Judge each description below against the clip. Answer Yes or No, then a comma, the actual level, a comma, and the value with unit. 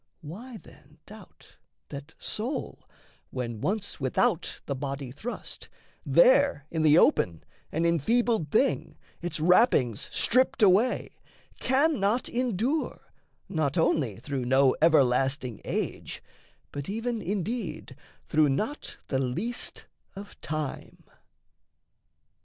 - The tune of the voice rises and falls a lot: Yes, wide, 8.9 semitones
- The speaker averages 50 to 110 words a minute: Yes, slow, 105 wpm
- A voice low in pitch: No, medium, 170 Hz